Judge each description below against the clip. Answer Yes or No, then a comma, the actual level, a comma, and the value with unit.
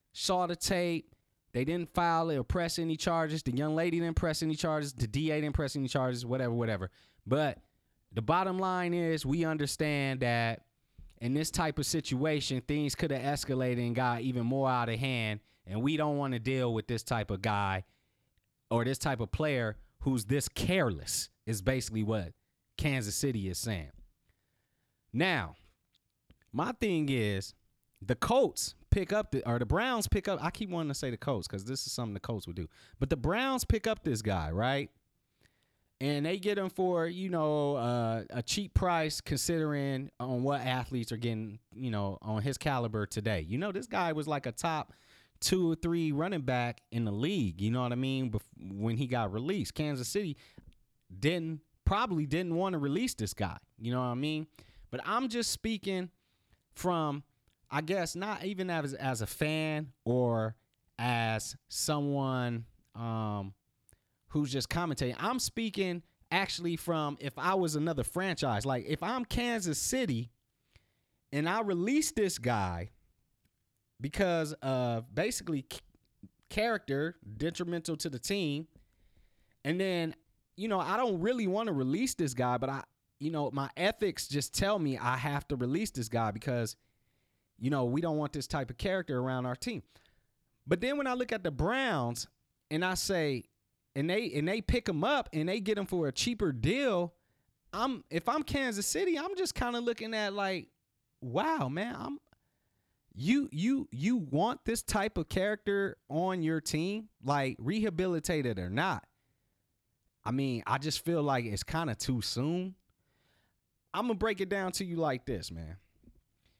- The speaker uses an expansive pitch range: Yes, wide, 6.6 semitones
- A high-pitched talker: No, medium, 140 Hz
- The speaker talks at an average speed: Yes, average, 175 wpm